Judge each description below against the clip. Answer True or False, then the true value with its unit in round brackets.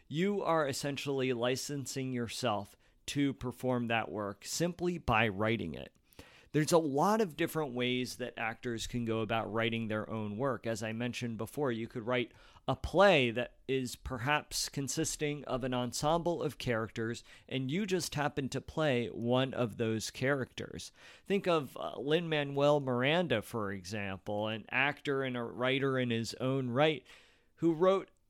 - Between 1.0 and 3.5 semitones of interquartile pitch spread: False (4.3 semitones)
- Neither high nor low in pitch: False (125 Hz)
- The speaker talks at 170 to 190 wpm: False (155 wpm)